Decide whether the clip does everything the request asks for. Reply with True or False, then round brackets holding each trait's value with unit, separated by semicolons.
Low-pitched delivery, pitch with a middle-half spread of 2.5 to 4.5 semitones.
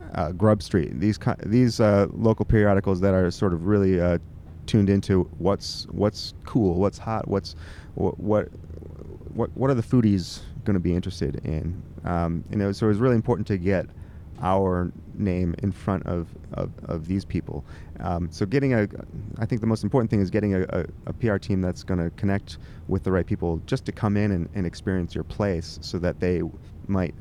True (95 Hz; 3.6 semitones)